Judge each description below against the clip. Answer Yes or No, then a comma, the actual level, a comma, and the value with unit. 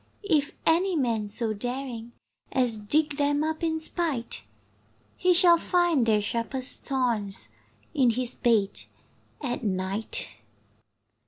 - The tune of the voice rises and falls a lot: Yes, wide, 5.8 semitones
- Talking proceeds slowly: Yes, slow, 115 wpm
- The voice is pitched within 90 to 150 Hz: No, very high, 255 Hz